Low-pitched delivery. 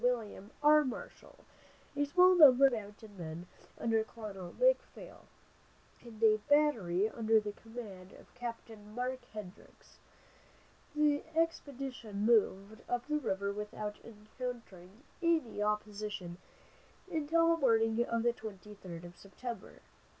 No: high, 225 Hz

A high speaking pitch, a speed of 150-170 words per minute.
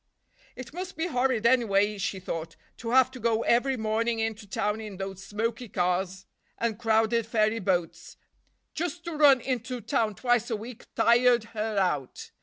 Yes: high, 225 Hz; average, 165 wpm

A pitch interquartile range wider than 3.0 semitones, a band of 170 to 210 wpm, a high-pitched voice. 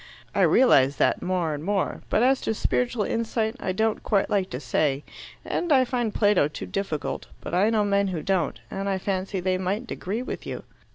Yes: average, 3.5 semitones; fast, 205 wpm; high, 195 Hz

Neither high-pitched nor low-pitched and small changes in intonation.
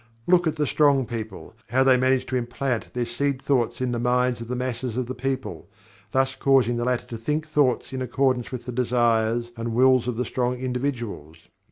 No: low, 125 Hz; narrow, 1.8 semitones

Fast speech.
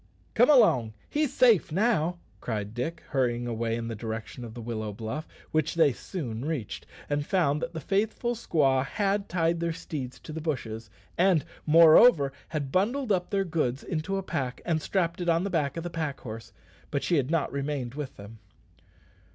No: average, 185 wpm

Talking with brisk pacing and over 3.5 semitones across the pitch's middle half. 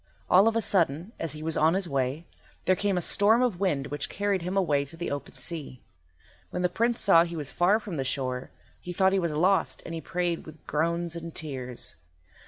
Yes: fast, 225 wpm; average, 4.1 semitones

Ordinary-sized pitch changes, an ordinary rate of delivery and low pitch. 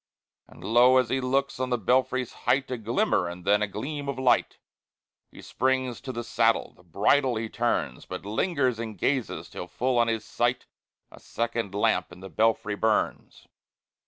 Yes: average, 3.5 semitones; average, 180 wpm; low, 120 Hz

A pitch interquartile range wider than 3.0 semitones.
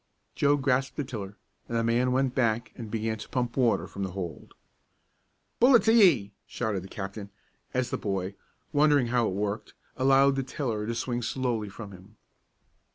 Yes: average, 4.1 semitones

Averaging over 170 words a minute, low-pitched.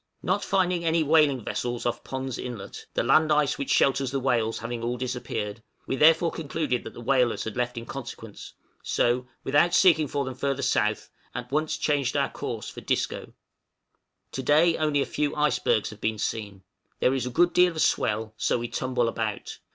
Yes: average, 190 wpm; low, 130 Hz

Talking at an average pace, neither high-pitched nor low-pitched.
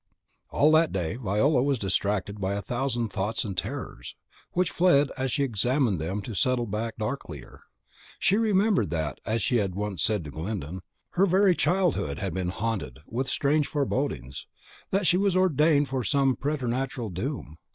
No: average, 170 wpm; low, 120 Hz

